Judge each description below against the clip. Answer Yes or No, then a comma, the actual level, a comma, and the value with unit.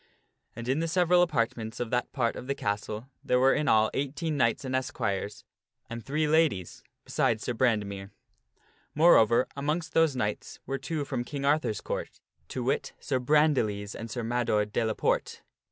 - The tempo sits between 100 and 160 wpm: No, average, 175 wpm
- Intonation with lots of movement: No, average, 5.0 semitones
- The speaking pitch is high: No, low, 125 Hz